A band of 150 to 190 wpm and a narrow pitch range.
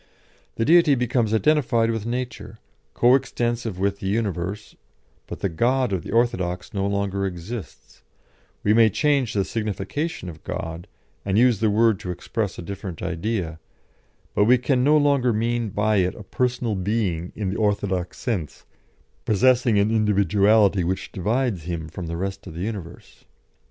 No: average, 160 wpm; average, 4.0 semitones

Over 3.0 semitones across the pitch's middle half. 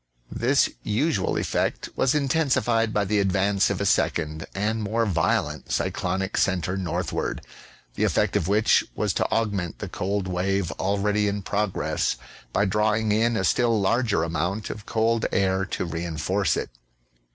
No: average, 2.7 semitones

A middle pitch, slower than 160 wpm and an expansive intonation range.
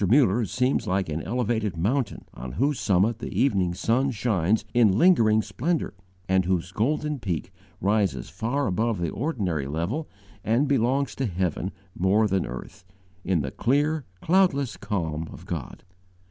No: low, 110 Hz; average, 145 wpm; wide, 6.3 semitones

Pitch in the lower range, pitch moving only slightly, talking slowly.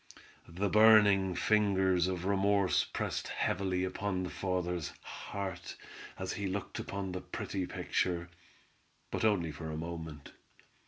Yes: very low, 95 Hz; narrow, 2.3 semitones; slow, 120 wpm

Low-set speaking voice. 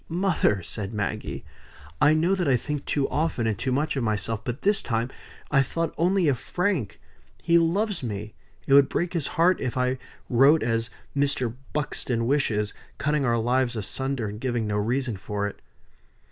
Yes: low, 130 Hz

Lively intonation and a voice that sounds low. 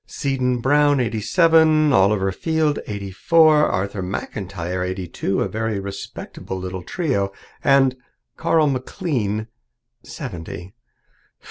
Yes: wide, 7.4 semitones; low, 110 Hz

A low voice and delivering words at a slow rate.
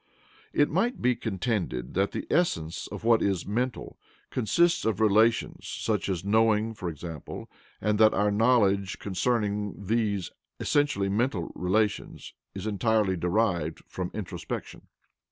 Yes: low, 105 Hz; slow, 130 wpm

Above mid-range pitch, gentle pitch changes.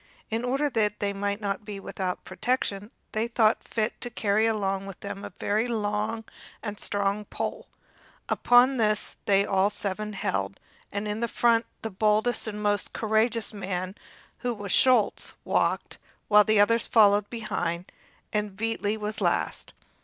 Yes: high, 210 Hz; narrow, 2.0 semitones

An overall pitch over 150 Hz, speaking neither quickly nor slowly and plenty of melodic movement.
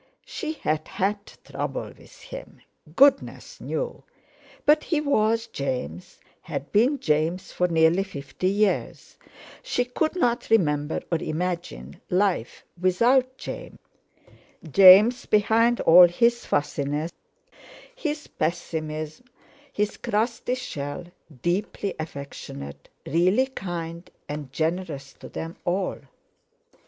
No: medium, 185 Hz; slow, 100 wpm; wide, 7.1 semitones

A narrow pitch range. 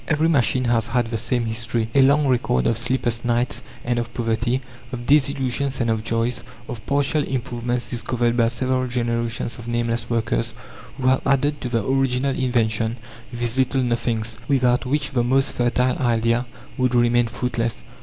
Yes: narrow, 1.8 semitones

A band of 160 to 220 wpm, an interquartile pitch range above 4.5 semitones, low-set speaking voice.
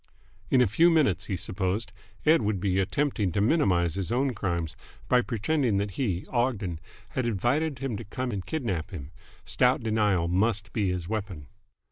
Yes: average, 170 wpm; average, 5.1 semitones; low, 105 Hz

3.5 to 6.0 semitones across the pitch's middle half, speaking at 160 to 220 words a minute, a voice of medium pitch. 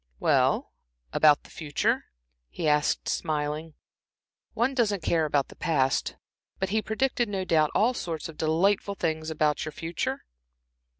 No: average, 4.7 semitones; average, 140 wpm; medium, 160 Hz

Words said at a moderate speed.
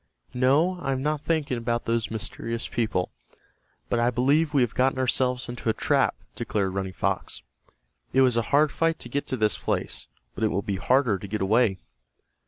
Yes: average, 190 wpm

